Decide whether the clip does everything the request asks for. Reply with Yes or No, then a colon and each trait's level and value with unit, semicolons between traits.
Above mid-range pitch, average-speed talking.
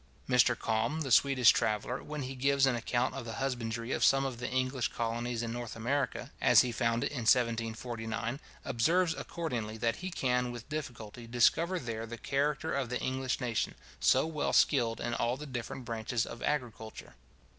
No: low, 125 Hz; average, 180 wpm